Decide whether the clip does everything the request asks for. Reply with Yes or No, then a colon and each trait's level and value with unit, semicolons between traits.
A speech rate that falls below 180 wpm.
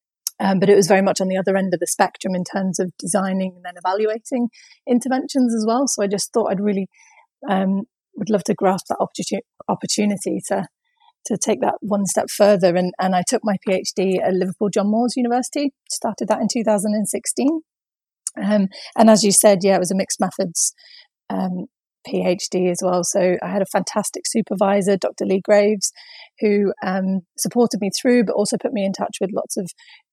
No: average, 190 wpm